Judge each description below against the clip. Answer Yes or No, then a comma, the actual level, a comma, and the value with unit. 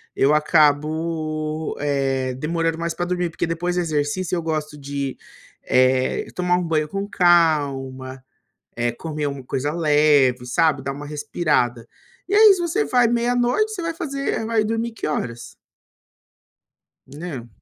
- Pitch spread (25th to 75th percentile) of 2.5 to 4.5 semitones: Yes, average, 4.2 semitones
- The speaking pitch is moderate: Yes, medium, 155 Hz